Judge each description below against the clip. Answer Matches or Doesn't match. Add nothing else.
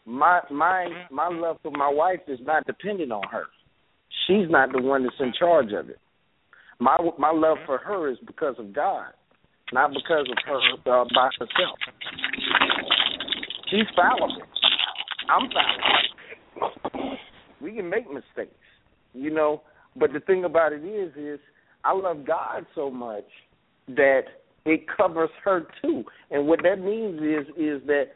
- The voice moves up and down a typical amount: Matches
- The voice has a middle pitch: Matches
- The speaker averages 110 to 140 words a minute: Doesn't match